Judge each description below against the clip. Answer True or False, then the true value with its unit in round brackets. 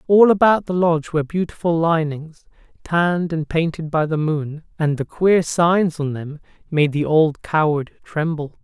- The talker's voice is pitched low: False (160 Hz)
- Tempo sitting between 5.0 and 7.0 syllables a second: False (4.5 syllables/s)